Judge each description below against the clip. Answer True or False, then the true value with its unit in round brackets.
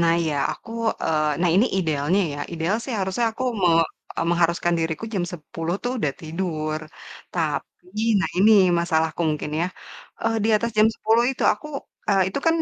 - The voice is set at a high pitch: False (175 Hz)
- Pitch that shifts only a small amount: False (4.6 semitones)